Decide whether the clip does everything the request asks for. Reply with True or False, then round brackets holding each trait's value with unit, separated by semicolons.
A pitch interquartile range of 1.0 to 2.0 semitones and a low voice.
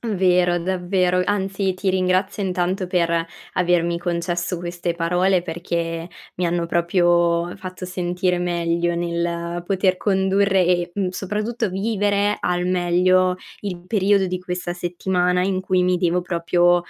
False (1.4 semitones; 180 Hz)